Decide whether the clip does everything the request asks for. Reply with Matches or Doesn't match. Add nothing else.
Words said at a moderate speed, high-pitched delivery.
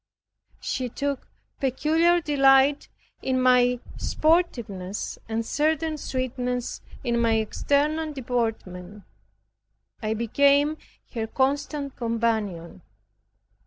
Doesn't match